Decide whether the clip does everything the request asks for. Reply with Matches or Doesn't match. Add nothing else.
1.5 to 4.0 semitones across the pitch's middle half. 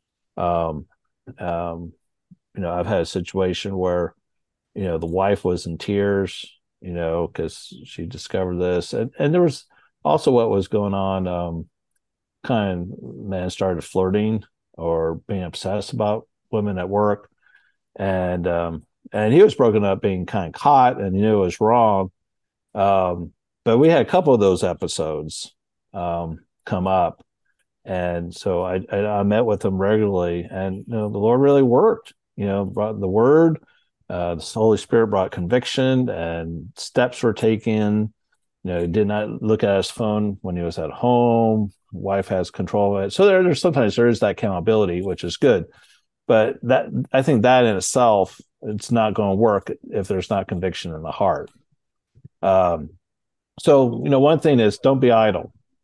Matches